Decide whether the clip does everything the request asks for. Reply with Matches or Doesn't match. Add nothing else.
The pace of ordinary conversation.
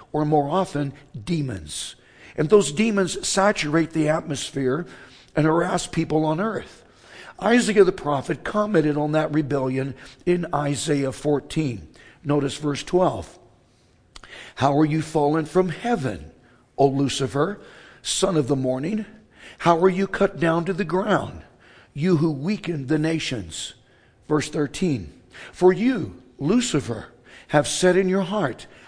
Doesn't match